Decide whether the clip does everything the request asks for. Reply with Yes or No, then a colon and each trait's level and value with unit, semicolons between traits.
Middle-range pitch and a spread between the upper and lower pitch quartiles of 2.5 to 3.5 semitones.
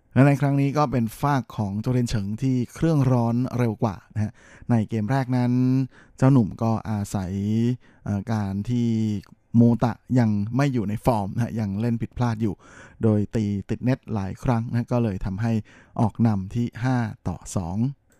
No: low, 115 Hz; average, 2.9 semitones